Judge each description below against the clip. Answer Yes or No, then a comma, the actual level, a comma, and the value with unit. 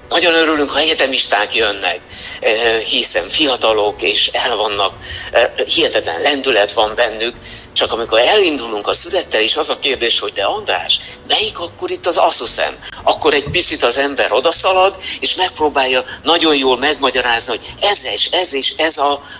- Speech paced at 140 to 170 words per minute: Yes, average, 150 wpm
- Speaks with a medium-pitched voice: Yes, medium, 170 Hz